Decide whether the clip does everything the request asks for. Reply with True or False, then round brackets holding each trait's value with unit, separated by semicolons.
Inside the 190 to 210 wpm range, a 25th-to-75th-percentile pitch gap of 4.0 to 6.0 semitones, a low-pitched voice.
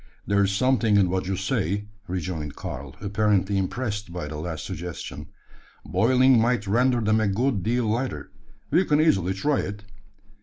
False (155 wpm; 4.7 semitones; 105 Hz)